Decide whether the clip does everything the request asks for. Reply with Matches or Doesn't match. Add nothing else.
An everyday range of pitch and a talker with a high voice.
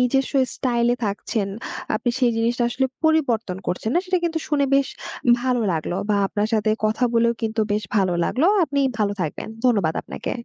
Matches